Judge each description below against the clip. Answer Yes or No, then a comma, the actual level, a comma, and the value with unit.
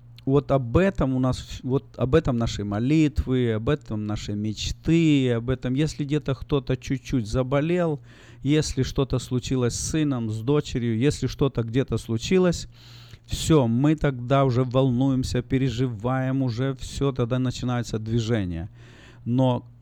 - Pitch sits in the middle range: No, low, 130 Hz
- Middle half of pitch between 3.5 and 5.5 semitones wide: No, average, 2.7 semitones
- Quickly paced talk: No, average, 135 wpm